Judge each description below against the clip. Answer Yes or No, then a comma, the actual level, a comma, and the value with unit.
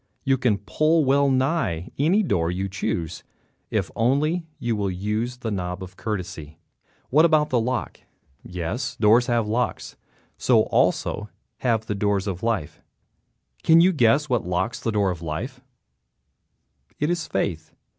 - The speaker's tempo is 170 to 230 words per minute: No, average, 145 wpm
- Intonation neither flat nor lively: No, wide, 6.2 semitones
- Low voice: Yes, low, 115 Hz